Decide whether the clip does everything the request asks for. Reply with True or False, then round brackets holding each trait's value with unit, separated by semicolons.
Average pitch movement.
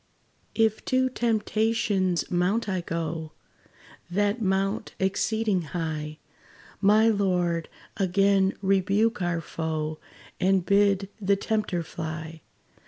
True (3.6 semitones)